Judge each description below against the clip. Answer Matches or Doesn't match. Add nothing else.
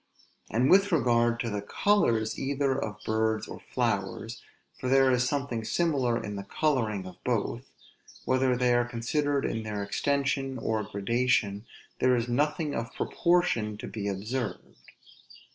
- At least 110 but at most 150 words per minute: Matches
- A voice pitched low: Matches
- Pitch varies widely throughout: Doesn't match